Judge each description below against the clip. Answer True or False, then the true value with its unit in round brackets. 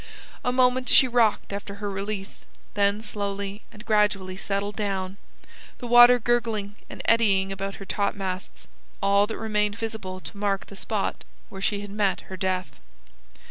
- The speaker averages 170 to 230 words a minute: False (155 wpm)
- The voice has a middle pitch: False (205 Hz)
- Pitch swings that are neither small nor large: False (1.9 semitones)